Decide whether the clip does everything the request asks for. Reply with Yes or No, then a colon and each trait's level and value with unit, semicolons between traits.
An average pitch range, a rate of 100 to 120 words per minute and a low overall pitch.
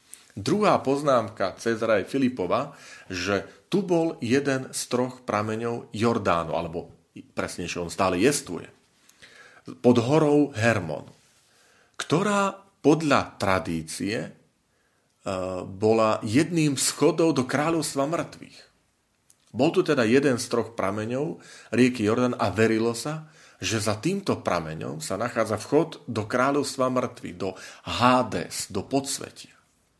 No: wide, 5.9 semitones; slow, 110 wpm; low, 120 Hz